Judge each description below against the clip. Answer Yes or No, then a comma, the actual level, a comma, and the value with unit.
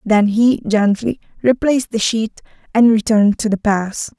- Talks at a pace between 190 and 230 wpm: No, average, 160 wpm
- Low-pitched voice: No, high, 220 Hz